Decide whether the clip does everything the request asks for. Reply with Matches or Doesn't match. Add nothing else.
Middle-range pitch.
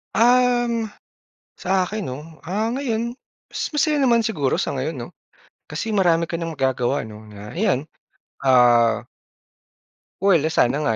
Matches